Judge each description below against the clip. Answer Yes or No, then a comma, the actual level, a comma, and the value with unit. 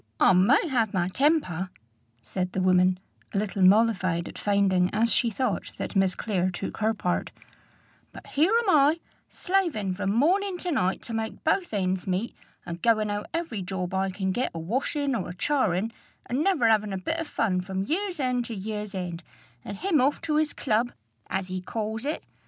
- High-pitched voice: Yes, high, 215 Hz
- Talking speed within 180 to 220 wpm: Yes, average, 190 wpm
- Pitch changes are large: Yes, wide, 6.7 semitones